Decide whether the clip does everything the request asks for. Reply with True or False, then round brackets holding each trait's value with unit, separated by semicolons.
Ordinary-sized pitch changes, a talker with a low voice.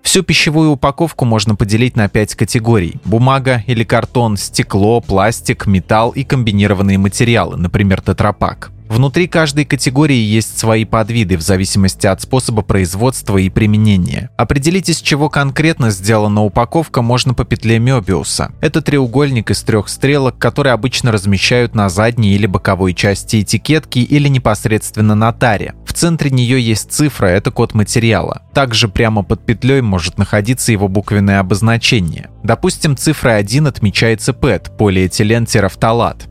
True (4.2 semitones; 115 Hz)